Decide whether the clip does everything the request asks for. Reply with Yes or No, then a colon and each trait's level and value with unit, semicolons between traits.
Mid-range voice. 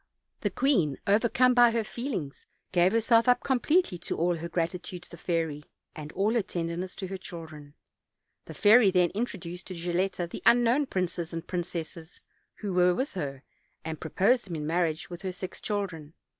Yes: medium, 180 Hz